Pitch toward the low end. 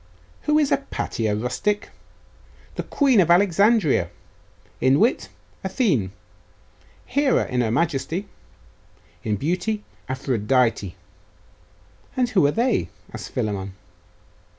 No: medium, 165 Hz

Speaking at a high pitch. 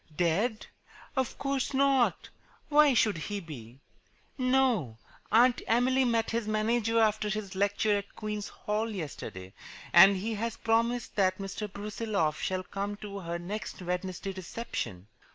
Yes: high, 210 Hz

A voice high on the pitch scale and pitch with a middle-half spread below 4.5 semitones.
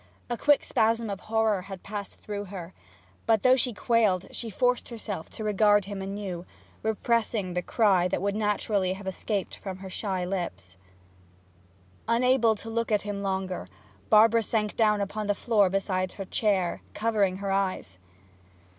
Yes: high, 205 Hz; average, 2.7 semitones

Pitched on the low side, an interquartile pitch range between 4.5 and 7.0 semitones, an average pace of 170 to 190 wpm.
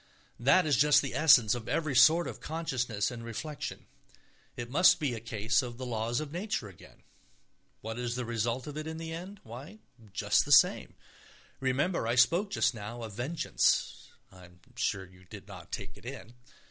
Yes: low, 125 Hz; average, 5.3 semitones; average, 185 wpm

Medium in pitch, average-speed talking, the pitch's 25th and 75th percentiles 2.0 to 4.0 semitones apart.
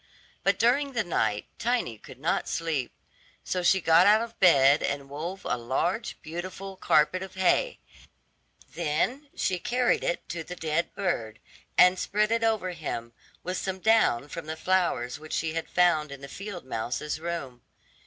No: medium, 170 Hz; average, 165 wpm; average, 4.7 semitones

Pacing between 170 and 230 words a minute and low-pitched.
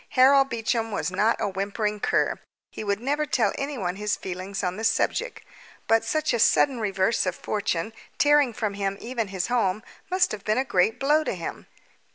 No: average, 190 wpm; high, 220 Hz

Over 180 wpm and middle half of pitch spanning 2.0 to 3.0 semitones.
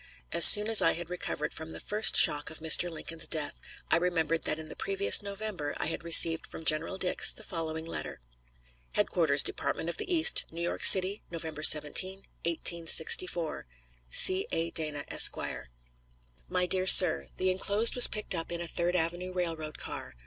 No: average, 175 wpm; narrow, 2.6 semitones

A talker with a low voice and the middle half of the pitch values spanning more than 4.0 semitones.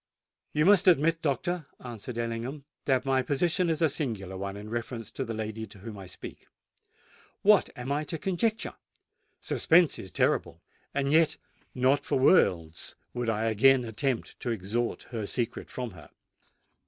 Yes: low, 125 Hz; average, 5.3 semitones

